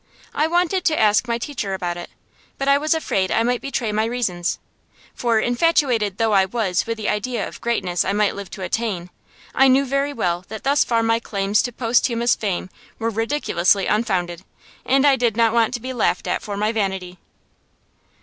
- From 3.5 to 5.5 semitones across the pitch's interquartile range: Yes, average, 4.1 semitones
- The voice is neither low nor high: No, high, 225 Hz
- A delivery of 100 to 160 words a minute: No, average, 200 wpm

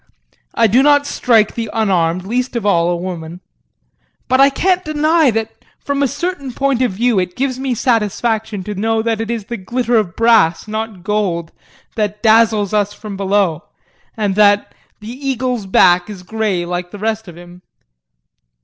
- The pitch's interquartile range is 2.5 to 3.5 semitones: No, average, 4.3 semitones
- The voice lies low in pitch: No, high, 220 Hz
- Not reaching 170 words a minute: No, average, 175 wpm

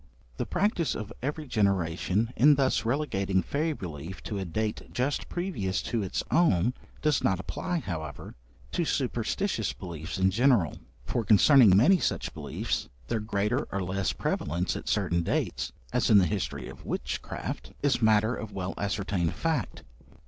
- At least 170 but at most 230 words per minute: No, average, 155 wpm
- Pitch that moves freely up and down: Yes, wide, 6.3 semitones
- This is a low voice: Yes, low, 105 Hz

